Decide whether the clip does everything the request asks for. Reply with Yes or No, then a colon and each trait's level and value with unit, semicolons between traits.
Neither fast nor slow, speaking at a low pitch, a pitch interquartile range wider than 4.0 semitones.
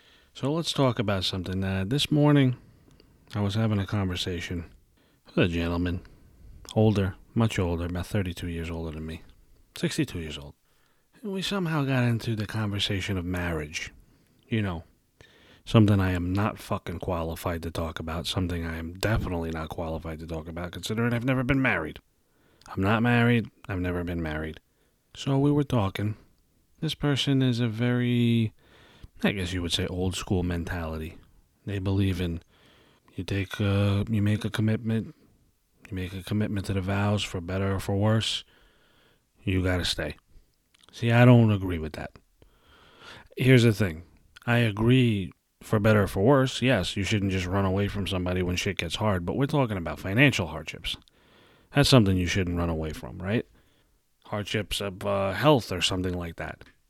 Yes: average, 170 wpm; low, 100 Hz; average, 4.4 semitones